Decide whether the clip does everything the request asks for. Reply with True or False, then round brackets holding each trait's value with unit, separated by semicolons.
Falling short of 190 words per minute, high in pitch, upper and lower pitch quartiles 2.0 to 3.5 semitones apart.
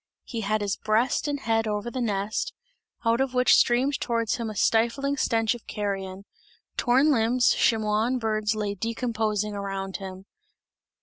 True (160 wpm; 225 Hz; 2.6 semitones)